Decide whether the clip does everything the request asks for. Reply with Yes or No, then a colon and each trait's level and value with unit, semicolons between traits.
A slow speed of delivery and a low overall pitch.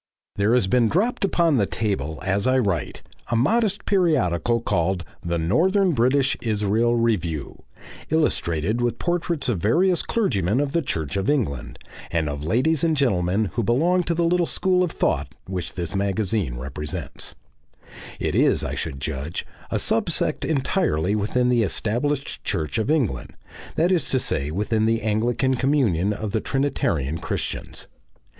No: average, 155 wpm; low, 115 Hz